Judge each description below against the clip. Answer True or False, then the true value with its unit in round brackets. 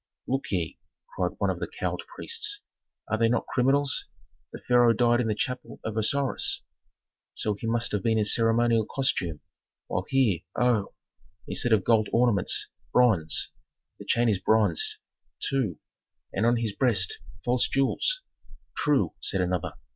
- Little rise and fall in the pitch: False (3.0 semitones)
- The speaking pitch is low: True (115 Hz)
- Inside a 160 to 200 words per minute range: False (150 wpm)